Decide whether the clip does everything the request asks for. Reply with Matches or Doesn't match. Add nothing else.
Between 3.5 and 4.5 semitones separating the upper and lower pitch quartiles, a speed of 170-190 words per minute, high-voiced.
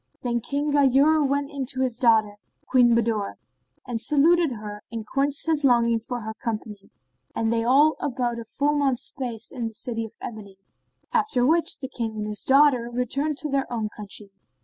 Matches